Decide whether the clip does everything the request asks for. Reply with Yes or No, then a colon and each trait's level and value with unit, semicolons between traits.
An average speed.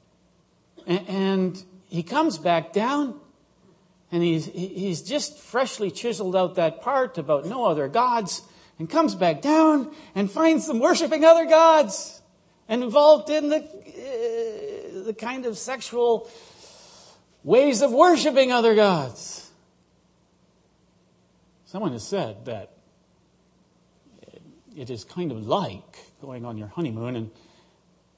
No: slow, 120 wpm